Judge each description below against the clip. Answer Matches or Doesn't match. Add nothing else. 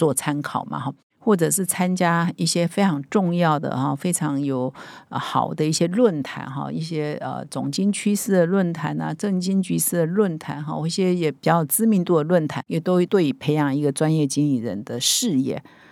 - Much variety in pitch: Doesn't match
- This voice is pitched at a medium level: Matches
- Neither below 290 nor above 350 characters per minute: Doesn't match